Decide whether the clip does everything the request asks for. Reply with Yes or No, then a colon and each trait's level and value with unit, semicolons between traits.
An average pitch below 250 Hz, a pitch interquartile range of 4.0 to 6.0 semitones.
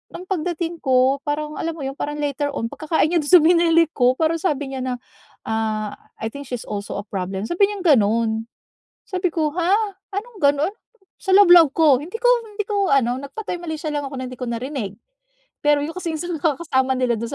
No: very high, 295 Hz; average, 5.1 semitones